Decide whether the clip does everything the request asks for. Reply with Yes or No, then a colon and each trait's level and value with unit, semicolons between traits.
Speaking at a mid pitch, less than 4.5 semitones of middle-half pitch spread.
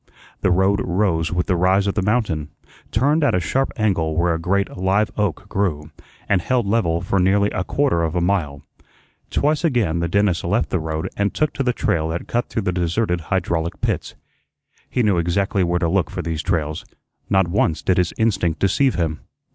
No: very low, 95 Hz; average, 3.5 semitones